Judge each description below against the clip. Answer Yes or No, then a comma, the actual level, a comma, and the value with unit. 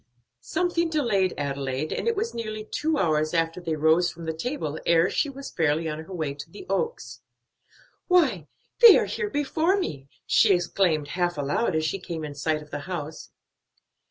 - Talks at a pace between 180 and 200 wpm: Yes, average, 185 wpm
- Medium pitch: Yes, medium, 170 Hz